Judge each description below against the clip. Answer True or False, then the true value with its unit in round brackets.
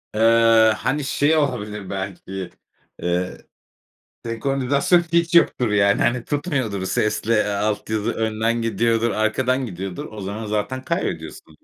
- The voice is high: False (115 Hz)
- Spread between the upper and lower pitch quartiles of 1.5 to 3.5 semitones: False (3.9 semitones)